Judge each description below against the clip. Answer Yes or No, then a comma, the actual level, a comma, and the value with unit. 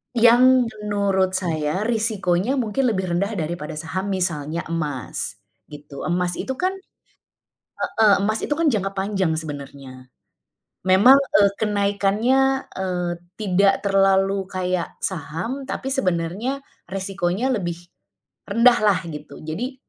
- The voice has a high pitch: Yes, high, 195 Hz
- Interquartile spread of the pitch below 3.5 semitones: No, average, 4.4 semitones